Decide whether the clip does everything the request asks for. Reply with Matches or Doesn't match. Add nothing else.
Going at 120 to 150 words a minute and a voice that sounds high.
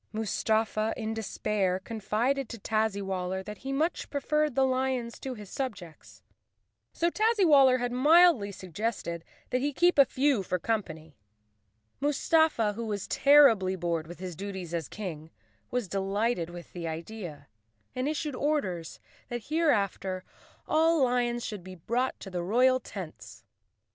Matches